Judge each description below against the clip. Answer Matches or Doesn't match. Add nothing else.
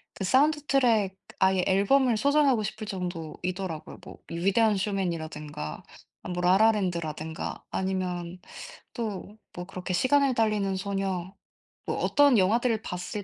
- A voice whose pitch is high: Matches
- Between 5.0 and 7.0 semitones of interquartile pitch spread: Doesn't match